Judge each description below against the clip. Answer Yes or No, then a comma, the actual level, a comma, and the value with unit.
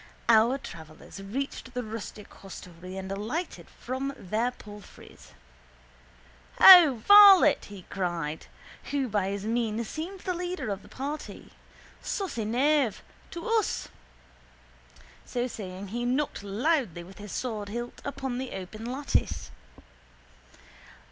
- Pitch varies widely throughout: Yes, wide, 5.7 semitones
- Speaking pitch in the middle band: No, high, 235 Hz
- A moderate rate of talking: No, slow, 115 wpm